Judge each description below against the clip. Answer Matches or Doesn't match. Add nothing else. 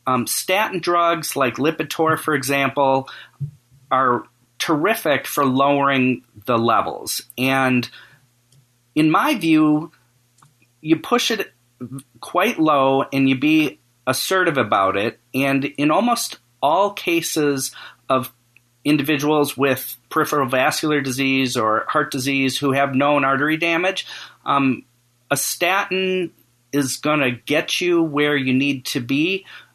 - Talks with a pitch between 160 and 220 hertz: Doesn't match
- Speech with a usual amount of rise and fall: Matches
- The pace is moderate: Doesn't match